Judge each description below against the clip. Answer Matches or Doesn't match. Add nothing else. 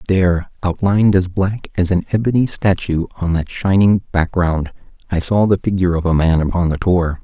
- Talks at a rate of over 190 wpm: Doesn't match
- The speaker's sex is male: Matches